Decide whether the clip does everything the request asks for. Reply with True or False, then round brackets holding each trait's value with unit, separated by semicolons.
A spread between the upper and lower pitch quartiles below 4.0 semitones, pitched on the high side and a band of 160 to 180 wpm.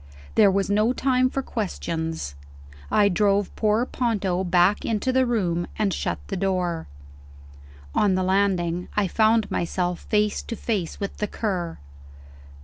False (3.3 semitones; 200 Hz; 145 wpm)